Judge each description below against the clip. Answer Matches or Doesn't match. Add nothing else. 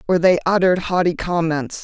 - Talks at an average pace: Matches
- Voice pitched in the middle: Matches